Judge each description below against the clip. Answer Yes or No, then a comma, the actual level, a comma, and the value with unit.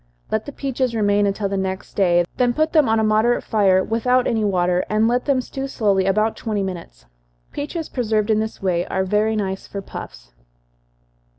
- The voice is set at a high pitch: Yes, high, 215 Hz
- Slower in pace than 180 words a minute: No, average, 190 wpm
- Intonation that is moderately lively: Yes, average, 3.8 semitones